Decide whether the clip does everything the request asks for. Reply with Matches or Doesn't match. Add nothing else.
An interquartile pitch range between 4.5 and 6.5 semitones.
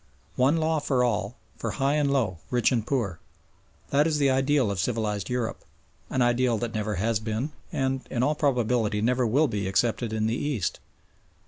Doesn't match